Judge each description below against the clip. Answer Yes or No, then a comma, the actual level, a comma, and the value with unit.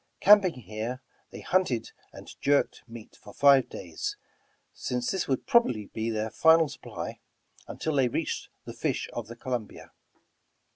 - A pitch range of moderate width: No, wide, 6.0 semitones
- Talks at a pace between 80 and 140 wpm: No, average, 150 wpm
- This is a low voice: Yes, low, 125 Hz